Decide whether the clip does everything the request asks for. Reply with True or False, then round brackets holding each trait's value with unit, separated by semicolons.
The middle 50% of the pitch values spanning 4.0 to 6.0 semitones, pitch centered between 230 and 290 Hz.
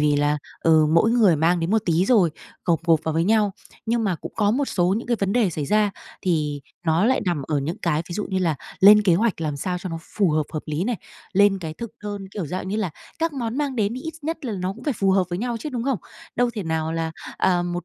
False (5.1 semitones; 190 Hz)